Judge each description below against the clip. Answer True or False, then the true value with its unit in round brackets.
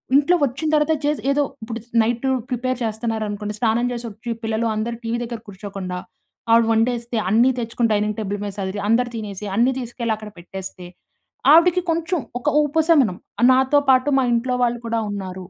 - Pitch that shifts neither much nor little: True (3.4 semitones)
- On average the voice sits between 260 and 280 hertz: False (230 Hz)